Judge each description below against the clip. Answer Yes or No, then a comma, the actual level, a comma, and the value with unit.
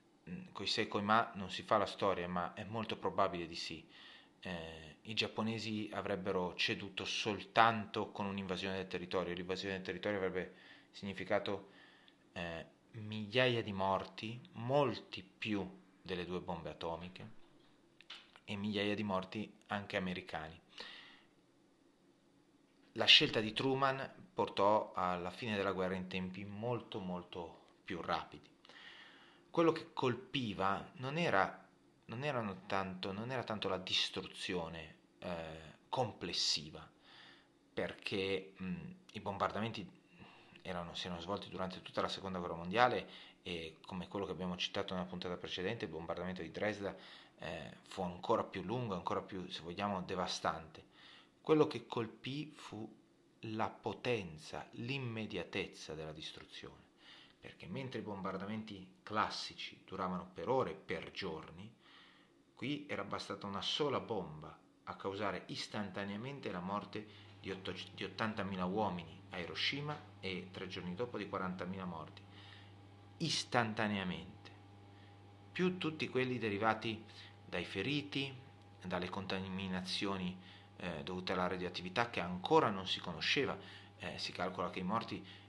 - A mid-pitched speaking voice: No, low, 100 Hz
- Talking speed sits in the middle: Yes, average, 125 wpm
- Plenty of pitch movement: No, average, 2.8 semitones